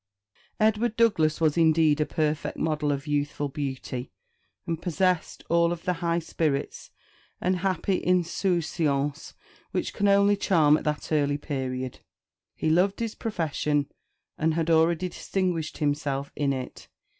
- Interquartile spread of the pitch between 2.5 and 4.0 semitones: Yes, average, 3.6 semitones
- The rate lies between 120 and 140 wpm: Yes, slow, 135 wpm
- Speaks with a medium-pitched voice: Yes, medium, 160 Hz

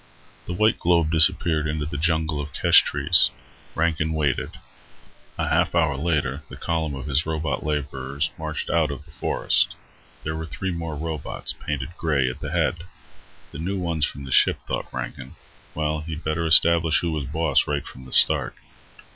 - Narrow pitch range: Yes, narrow, 2.2 semitones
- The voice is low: Yes, very low, 80 Hz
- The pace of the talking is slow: No, average, 175 wpm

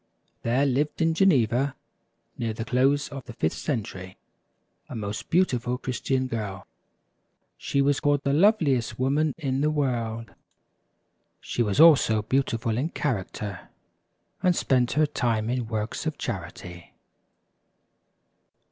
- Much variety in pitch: No, average, 4.2 semitones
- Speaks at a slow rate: Yes, slow, 125 wpm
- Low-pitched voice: Yes, low, 130 Hz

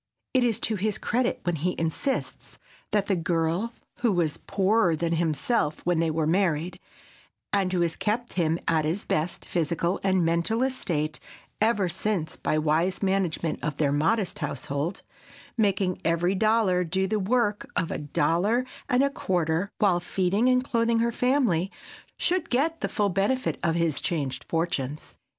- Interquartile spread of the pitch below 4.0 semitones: No, average, 4.8 semitones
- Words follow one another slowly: No, average, 155 wpm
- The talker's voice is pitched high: No, medium, 180 Hz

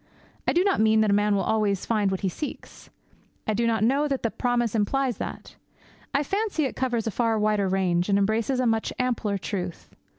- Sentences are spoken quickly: Yes, fast, 210 wpm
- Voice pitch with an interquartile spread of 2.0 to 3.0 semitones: No, average, 3.9 semitones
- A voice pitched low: No, high, 220 Hz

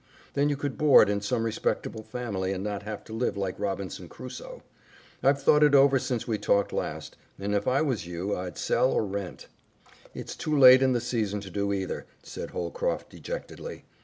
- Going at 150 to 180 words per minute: No, average, 190 wpm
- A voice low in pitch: Yes, low, 110 Hz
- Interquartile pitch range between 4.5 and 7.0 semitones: Yes, average, 5.1 semitones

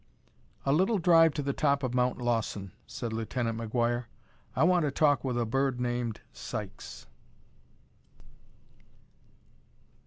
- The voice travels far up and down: No, average, 3.5 semitones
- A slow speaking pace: Yes, slow, 125 wpm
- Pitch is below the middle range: Yes, low, 125 Hz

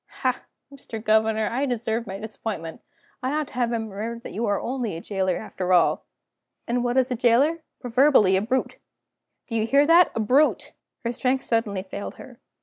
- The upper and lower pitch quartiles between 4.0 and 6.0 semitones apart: No, average, 3.2 semitones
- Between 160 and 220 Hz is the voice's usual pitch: No, high, 230 Hz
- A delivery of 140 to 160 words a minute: No, average, 185 wpm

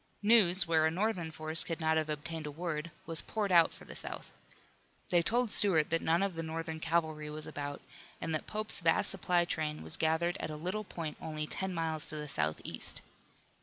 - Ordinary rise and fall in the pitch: No, narrow, 2.2 semitones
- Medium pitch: Yes, medium, 165 Hz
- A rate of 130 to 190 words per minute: No, fast, 205 wpm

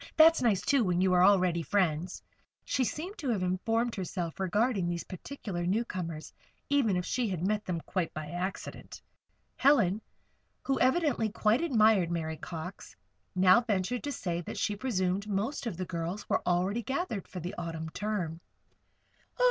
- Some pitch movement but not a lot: Yes, average, 4.8 semitones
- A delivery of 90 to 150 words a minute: No, average, 160 wpm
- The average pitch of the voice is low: No, high, 190 Hz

